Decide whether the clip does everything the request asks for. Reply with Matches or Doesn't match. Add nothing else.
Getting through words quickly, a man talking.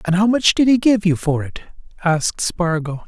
Matches